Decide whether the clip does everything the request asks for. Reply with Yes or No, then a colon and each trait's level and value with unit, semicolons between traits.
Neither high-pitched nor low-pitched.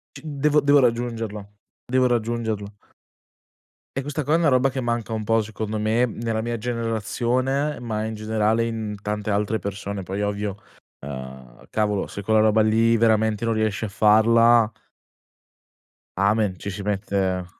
No: low, 110 Hz